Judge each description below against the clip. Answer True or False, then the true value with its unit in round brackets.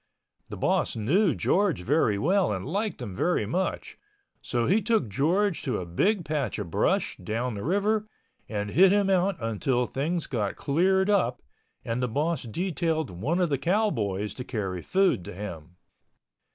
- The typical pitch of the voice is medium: True (145 Hz)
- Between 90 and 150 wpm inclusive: False (165 wpm)